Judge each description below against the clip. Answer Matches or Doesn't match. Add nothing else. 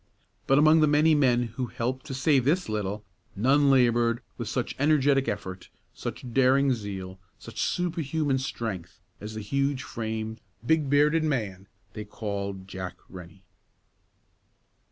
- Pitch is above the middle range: Doesn't match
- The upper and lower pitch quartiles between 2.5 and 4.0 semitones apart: Doesn't match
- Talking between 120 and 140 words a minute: Matches